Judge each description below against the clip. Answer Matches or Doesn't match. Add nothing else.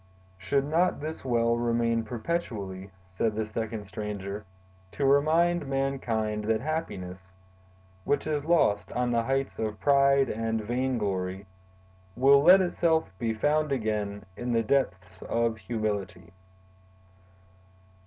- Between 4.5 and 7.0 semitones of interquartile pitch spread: Matches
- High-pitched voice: Doesn't match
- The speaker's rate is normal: Doesn't match